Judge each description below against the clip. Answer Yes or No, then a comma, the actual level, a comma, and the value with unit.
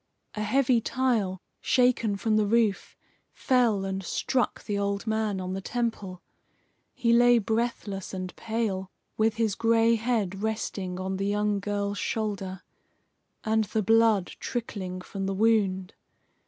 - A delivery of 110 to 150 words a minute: Yes, average, 140 wpm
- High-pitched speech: Yes, high, 210 Hz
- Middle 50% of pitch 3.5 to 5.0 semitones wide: No, average, 2.8 semitones